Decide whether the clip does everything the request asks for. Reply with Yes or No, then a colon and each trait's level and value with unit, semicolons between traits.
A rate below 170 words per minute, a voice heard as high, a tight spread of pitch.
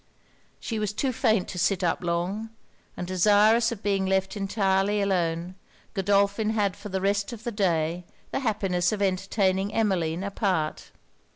Yes: average, 155 wpm; high, 195 Hz; narrow, 2.3 semitones